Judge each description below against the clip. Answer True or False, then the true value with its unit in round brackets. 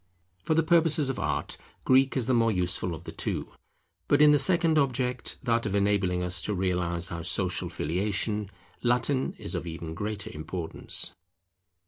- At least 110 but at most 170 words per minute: True (165 wpm)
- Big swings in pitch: True (6.7 semitones)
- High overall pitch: False (105 Hz)